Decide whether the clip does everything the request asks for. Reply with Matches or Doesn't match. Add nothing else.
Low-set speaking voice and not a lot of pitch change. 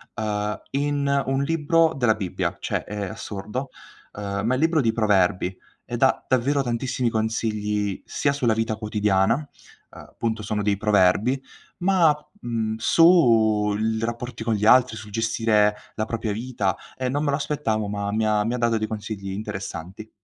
Doesn't match